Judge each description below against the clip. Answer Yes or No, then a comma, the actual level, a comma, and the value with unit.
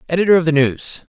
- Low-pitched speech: No, medium, 160 Hz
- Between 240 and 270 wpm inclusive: No, fast, 210 wpm